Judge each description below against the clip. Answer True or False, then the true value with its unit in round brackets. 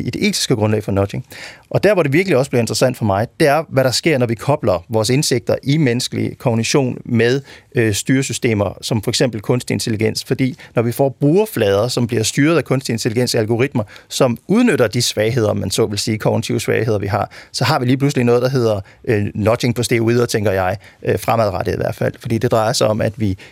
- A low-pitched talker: True (120 Hz)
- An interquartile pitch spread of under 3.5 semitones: True (3.0 semitones)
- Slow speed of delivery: False (225 wpm)